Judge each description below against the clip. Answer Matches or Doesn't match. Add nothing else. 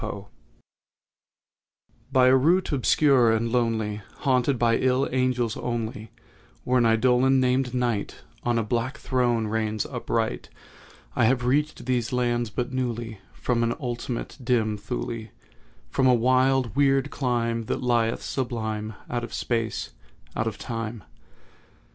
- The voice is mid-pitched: Doesn't match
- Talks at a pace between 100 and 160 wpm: Matches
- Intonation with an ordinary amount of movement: Doesn't match